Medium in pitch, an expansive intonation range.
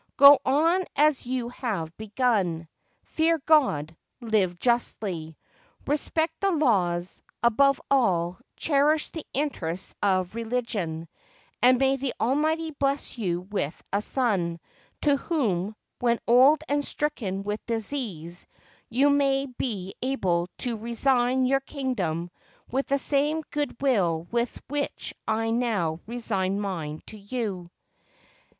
No: high, 235 Hz; wide, 6.7 semitones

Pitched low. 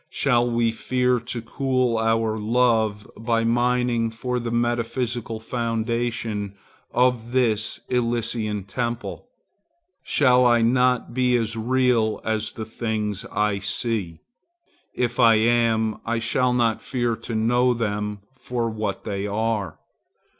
Yes: low, 115 Hz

